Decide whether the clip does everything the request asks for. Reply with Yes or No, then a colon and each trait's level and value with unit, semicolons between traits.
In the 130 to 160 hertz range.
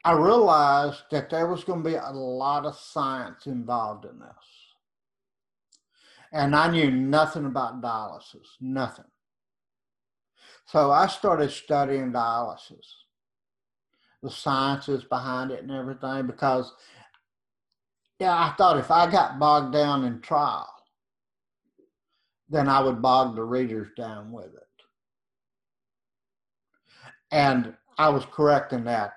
Yes: low, 135 Hz